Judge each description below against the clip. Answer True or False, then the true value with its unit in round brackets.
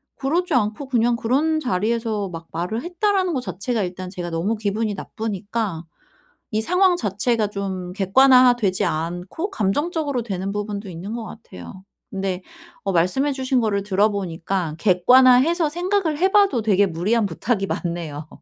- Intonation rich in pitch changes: True (5.8 semitones)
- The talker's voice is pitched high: True (215 Hz)